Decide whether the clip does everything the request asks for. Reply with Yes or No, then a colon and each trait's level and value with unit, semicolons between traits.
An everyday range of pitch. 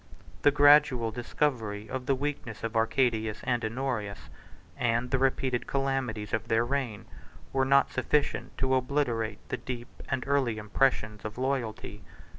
Yes: average, 3.3 semitones